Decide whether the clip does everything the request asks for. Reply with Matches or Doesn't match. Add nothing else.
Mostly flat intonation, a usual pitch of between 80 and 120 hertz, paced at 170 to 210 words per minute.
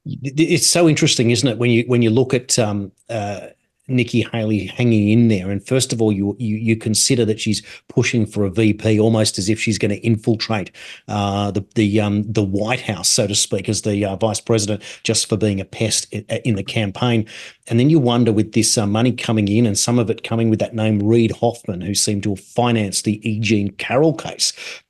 Doesn't match